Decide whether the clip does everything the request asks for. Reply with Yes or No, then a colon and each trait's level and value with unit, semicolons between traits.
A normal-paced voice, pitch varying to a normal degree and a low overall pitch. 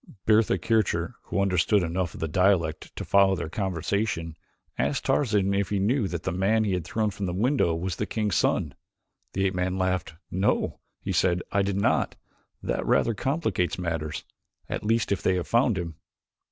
Yes: average, 185 wpm; average, 3.0 semitones; very low, 95 Hz